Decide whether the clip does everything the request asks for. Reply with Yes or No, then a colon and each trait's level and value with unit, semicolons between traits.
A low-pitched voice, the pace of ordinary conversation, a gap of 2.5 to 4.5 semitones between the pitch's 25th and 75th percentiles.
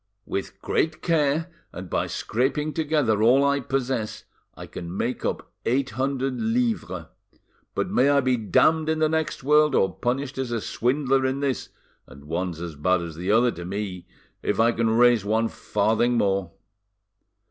No: low, 120 Hz; average, 170 wpm; average, 5.0 semitones